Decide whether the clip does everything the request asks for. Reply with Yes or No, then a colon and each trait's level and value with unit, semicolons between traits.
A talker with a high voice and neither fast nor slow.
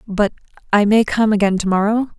Yes: high, 210 Hz; average, 165 wpm